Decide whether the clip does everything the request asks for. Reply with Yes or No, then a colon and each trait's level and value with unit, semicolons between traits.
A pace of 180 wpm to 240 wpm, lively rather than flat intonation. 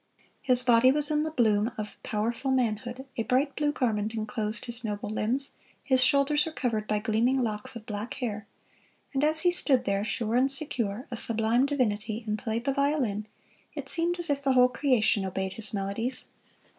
No: average, 185 wpm; average, 4.2 semitones